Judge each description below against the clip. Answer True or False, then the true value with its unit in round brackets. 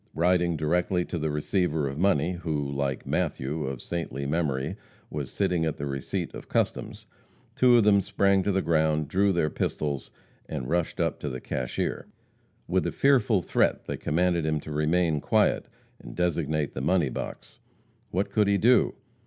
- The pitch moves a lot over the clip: False (3.8 semitones)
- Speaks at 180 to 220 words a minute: False (170 wpm)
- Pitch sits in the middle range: False (80 Hz)